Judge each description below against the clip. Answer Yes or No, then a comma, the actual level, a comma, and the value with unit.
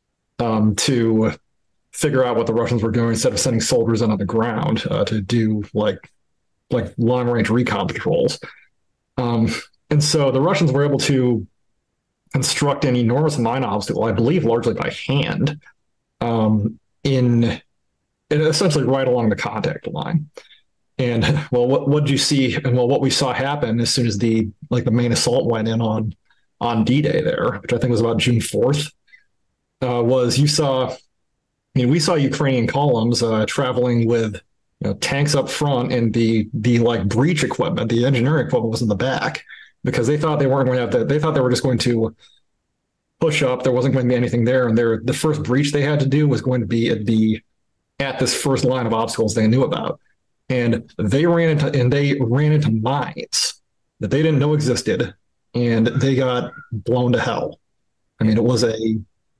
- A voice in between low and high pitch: No, low, 125 Hz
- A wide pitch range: No, average, 3.3 semitones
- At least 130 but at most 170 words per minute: No, average, 195 wpm